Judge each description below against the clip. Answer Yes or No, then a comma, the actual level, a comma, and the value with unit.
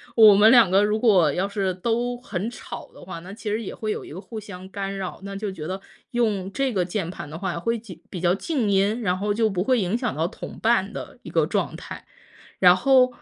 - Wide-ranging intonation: No, average, 3.4 semitones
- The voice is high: Yes, high, 200 Hz